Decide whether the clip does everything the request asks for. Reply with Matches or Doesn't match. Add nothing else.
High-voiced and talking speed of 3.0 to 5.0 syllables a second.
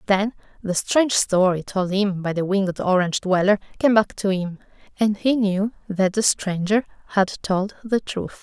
Matches